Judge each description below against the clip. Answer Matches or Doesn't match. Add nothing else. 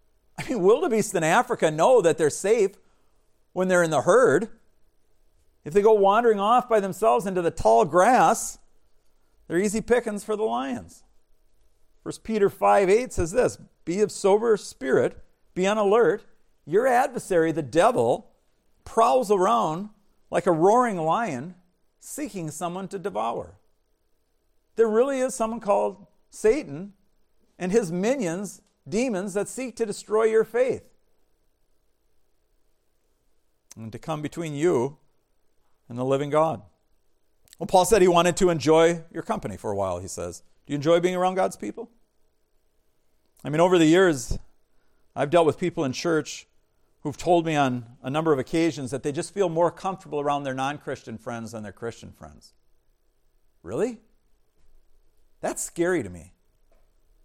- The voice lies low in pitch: Doesn't match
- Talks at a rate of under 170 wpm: Matches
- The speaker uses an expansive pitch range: Matches